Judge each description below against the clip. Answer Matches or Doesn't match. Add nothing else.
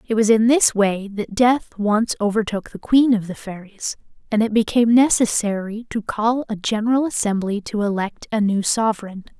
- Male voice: Doesn't match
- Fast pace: Doesn't match